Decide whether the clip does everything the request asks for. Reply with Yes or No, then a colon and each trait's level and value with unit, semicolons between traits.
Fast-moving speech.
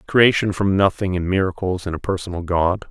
No: average, 185 wpm